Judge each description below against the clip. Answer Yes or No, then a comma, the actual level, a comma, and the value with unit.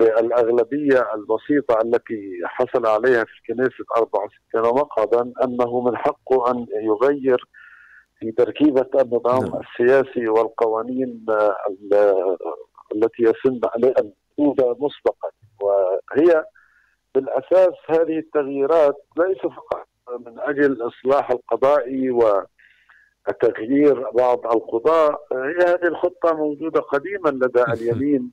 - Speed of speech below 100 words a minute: Yes, average, 90 wpm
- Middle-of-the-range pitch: No, low, 130 Hz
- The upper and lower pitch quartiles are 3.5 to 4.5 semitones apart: Yes, average, 3.8 semitones